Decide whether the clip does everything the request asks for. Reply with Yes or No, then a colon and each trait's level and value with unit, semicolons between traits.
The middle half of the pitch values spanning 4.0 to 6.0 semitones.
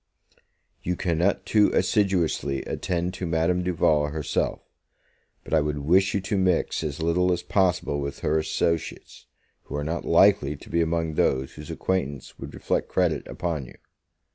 No: average, 3.3 semitones